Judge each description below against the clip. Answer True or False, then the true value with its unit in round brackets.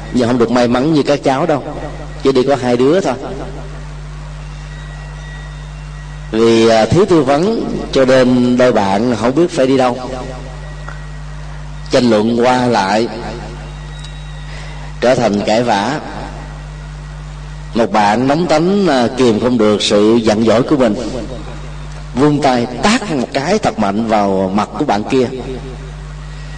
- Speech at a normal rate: False (135 wpm)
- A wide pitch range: False (3.6 semitones)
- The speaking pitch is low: False (145 Hz)